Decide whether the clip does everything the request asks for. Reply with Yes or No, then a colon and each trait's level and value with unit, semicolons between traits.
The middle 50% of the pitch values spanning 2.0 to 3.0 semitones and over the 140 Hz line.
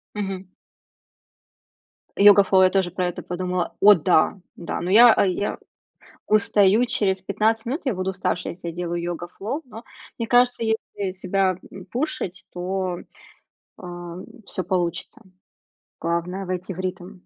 Yes: average, 2.7 semitones; high, 190 Hz